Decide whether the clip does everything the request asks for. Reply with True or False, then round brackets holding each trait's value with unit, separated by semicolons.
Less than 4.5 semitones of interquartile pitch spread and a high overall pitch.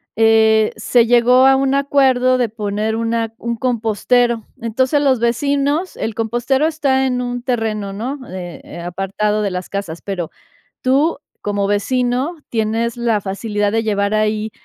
True (3.3 semitones; 230 Hz)